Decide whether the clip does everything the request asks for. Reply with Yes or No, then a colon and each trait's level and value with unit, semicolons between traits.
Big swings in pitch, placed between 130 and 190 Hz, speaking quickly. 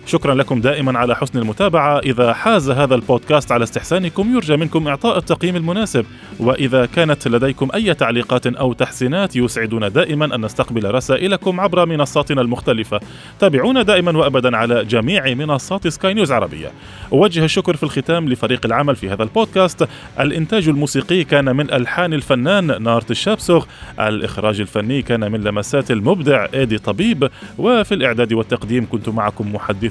Yes: wide, 6.1 semitones; low, 135 Hz; fast, 145 wpm